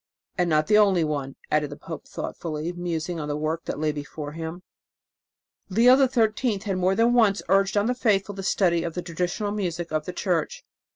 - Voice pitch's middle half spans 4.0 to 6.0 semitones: Yes, average, 4.3 semitones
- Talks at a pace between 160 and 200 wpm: Yes, average, 195 wpm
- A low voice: No, medium, 180 Hz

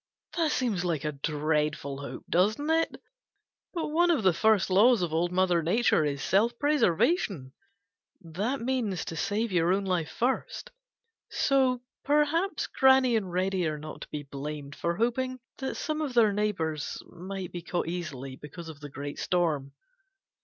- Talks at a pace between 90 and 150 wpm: No, average, 160 wpm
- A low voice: No, medium, 185 Hz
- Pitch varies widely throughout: Yes, wide, 7.7 semitones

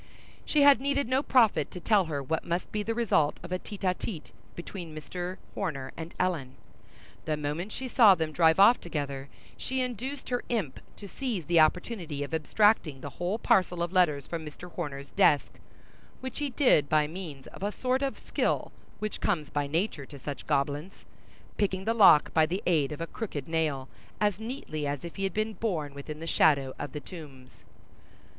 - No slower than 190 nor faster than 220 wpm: Yes, average, 195 wpm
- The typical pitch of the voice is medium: Yes, medium, 170 Hz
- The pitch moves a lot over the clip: Yes, wide, 6.1 semitones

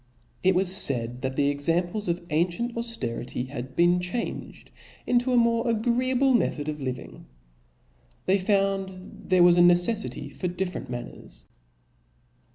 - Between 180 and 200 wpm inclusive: No, average, 150 wpm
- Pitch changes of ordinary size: No, wide, 7.4 semitones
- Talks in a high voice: No, medium, 180 Hz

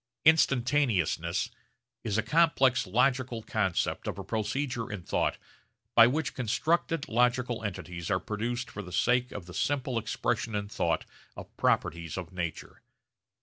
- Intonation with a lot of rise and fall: No, average, 4.3 semitones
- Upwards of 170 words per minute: No, average, 140 wpm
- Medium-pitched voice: No, low, 115 Hz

